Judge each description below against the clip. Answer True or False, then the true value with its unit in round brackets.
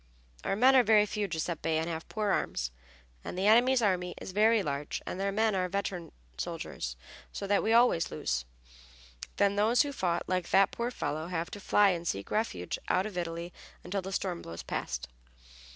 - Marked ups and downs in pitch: False (3.9 semitones)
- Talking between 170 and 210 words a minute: True (190 wpm)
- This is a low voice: False (190 Hz)